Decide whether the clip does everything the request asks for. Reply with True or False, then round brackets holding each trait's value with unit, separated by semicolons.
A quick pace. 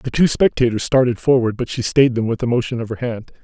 True (260 wpm)